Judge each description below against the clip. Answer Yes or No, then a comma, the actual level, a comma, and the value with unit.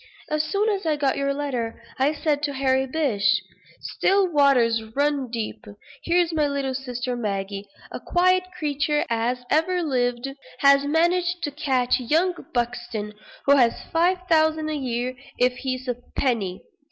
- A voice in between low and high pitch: No, very high, 275 Hz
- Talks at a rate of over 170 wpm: No, average, 155 wpm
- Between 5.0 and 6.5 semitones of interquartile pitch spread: No, average, 4.2 semitones